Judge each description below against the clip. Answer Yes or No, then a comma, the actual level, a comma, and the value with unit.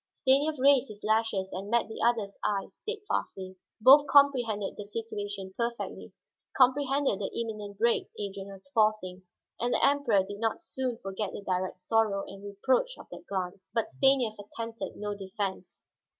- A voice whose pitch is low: No, high, 215 Hz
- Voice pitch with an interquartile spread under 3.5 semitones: No, average, 4.3 semitones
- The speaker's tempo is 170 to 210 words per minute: No, average, 155 wpm